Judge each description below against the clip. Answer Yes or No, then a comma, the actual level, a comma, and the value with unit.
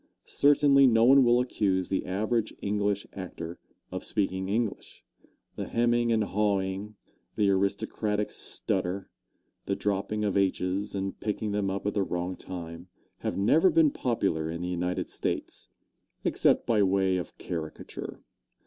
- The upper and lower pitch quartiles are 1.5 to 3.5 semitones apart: Yes, average, 2.7 semitones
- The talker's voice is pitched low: Yes, low, 100 Hz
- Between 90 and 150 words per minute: Yes, average, 140 wpm